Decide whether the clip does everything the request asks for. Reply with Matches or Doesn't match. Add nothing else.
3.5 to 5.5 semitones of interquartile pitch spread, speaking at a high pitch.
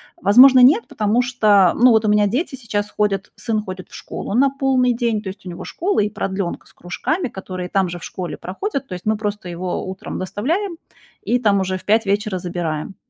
Matches